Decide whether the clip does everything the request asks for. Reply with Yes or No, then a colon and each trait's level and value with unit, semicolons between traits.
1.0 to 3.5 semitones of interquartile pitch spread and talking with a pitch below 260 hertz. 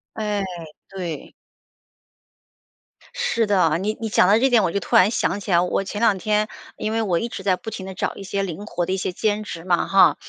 Yes: average, 2.7 semitones; high, 195 Hz